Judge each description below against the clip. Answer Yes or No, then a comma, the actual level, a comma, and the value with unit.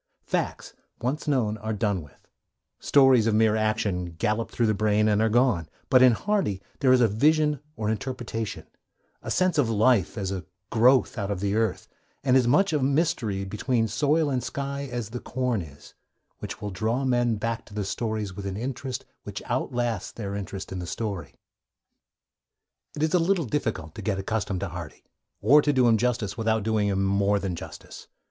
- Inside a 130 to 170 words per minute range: No, average, 190 wpm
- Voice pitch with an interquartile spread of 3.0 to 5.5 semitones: Yes, average, 4.2 semitones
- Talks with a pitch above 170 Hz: No, low, 110 Hz